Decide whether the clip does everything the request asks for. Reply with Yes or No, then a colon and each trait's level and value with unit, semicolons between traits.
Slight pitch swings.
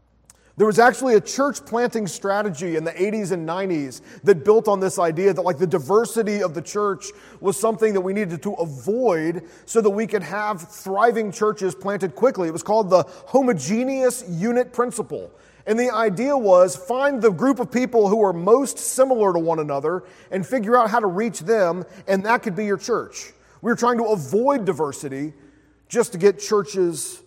No: average, 4.3 semitones